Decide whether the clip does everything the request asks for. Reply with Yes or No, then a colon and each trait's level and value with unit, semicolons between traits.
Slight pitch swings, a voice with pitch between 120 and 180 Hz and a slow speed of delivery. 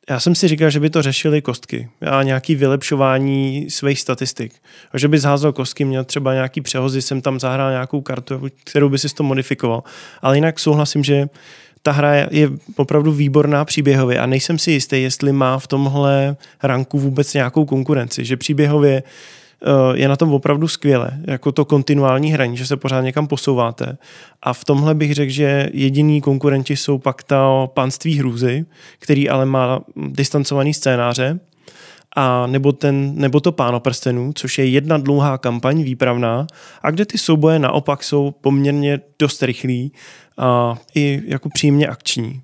No: narrow, 2.0 semitones; medium, 140 Hz; average, 165 wpm